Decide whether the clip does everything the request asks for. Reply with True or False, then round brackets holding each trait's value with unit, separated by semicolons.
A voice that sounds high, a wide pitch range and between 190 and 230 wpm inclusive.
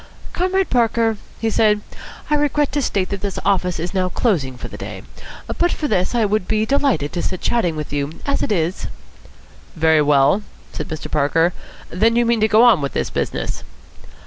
True (205 Hz; 6.4 semitones; 200 wpm)